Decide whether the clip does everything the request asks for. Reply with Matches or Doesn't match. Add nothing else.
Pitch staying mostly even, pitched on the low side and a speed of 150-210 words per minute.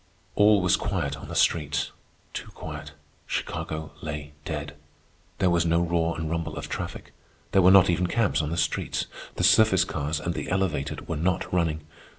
Doesn't match